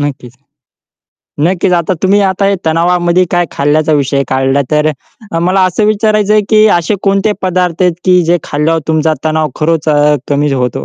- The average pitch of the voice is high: No, medium, 165 Hz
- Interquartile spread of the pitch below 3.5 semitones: No, average, 3.8 semitones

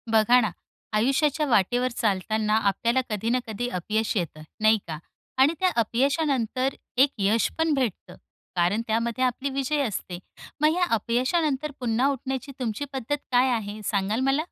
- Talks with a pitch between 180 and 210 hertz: No, high, 240 Hz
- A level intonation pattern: No, average, 3.8 semitones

